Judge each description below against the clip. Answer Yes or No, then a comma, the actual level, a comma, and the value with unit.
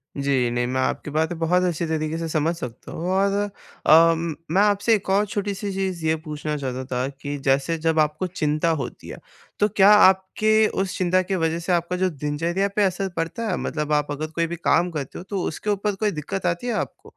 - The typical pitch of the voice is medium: Yes, medium, 170 Hz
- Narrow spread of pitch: No, average, 4.0 semitones